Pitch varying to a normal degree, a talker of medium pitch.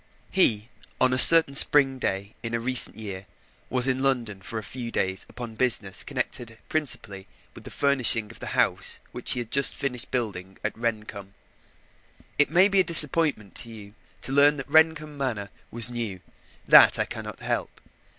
No: average, 4.6 semitones; low, 120 Hz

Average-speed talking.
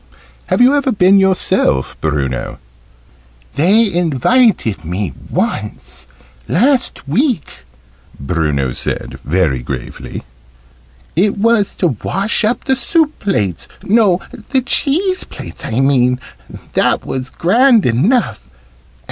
No: slow, 105 wpm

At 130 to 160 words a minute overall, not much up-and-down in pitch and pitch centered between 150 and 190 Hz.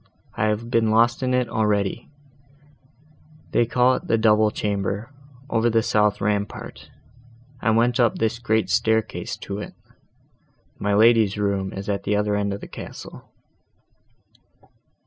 No: average, 145 wpm; narrow, 2.1 semitones; low, 110 Hz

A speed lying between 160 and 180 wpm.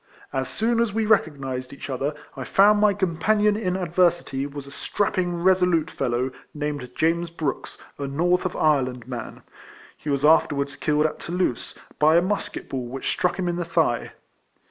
Yes: average, 175 wpm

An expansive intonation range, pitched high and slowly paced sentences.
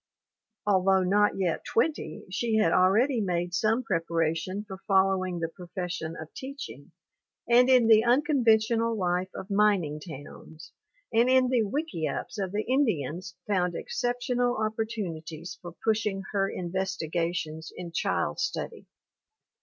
No: average, 4.6 semitones; high, 195 Hz; slow, 130 wpm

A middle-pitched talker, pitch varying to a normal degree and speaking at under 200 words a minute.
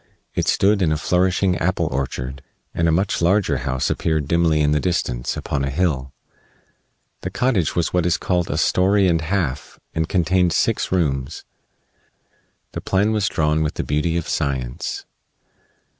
No: very low, 85 Hz; average, 4.1 semitones; average, 160 wpm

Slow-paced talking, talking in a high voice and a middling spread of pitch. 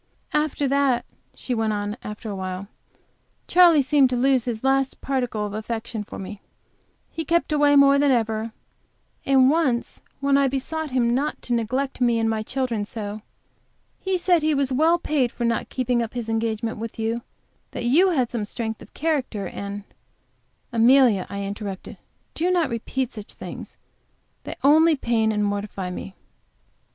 No: average, 165 wpm; high, 245 Hz; average, 4.2 semitones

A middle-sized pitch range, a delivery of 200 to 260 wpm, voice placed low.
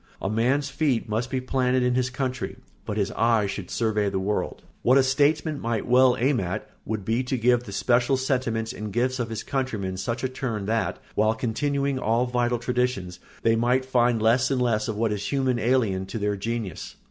Yes: average, 3.1 semitones; fast, 205 wpm; low, 120 Hz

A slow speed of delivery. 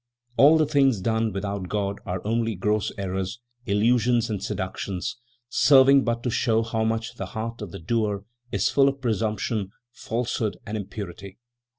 No: average, 160 wpm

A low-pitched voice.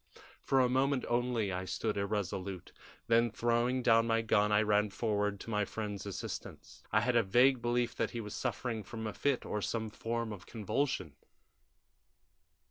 Yes: low, 115 Hz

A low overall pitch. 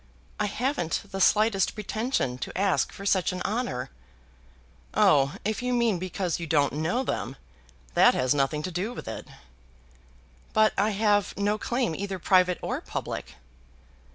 No: high, 195 Hz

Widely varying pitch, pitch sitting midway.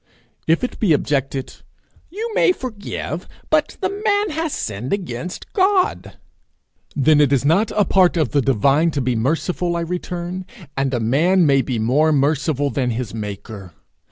Yes: wide, 6.3 semitones; medium, 155 Hz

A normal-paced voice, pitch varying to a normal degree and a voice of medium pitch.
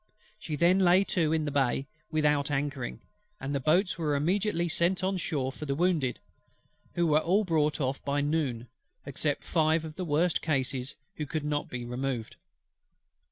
Yes: average, 170 wpm; average, 3.5 semitones; medium, 150 Hz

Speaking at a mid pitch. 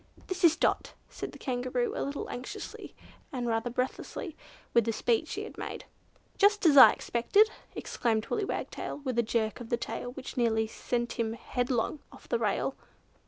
No: high, 245 Hz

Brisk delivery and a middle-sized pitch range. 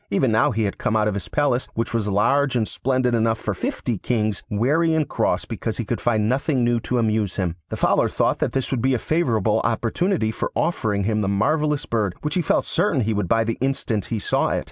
Yes: fast, 235 wpm; average, 4.0 semitones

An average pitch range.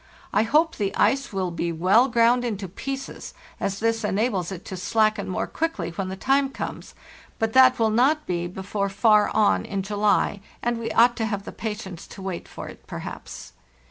Yes: average, 3.8 semitones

